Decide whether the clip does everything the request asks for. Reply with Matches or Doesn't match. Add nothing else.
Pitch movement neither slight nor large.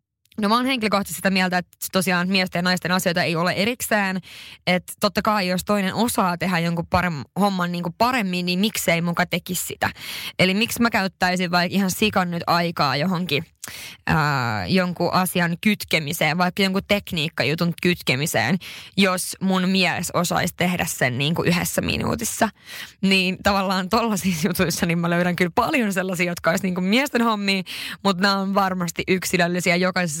Doesn't match